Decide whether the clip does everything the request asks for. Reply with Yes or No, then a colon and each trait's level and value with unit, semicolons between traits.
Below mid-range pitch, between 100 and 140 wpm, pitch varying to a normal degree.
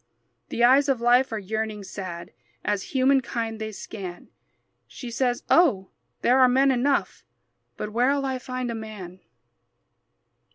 No: high, 235 Hz; slow, 135 wpm; average, 3.7 semitones